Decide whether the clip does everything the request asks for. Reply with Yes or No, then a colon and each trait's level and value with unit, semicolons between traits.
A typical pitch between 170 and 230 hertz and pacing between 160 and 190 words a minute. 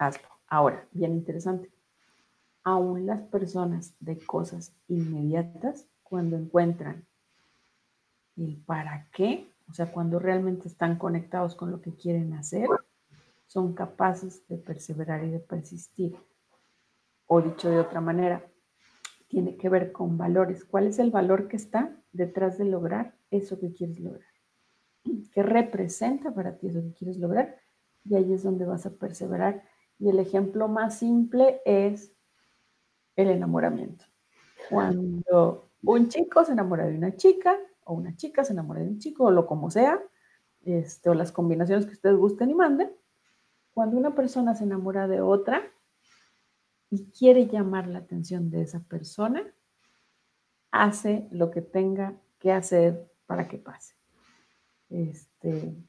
No: medium, 185 Hz; average, 140 wpm